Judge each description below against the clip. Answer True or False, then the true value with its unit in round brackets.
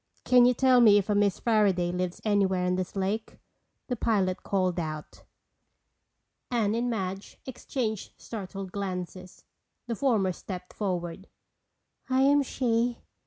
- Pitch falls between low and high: False (200 Hz)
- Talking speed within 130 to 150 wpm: True (135 wpm)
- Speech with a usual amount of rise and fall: True (4.1 semitones)